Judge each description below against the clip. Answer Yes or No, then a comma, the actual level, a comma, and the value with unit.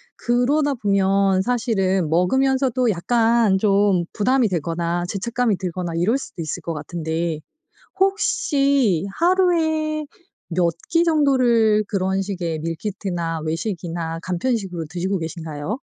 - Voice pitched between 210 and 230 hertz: No, high, 195 Hz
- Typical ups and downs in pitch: No, wide, 6.4 semitones